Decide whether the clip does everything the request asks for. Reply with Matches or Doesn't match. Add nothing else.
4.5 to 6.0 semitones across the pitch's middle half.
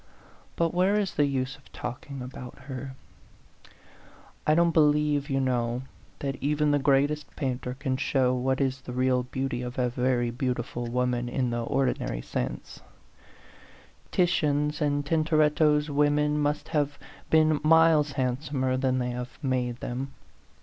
Doesn't match